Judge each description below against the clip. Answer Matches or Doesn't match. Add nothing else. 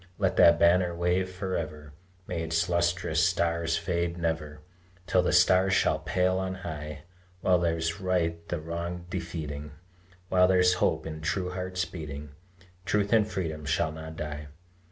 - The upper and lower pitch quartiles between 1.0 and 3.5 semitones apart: Matches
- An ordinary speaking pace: Matches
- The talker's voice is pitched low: Matches